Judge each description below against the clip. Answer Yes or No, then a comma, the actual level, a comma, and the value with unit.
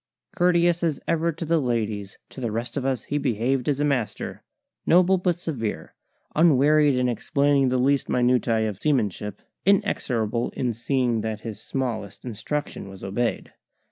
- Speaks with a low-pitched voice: Yes, low, 125 Hz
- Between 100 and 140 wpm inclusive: No, average, 155 wpm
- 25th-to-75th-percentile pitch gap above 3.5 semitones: Yes, average, 4.8 semitones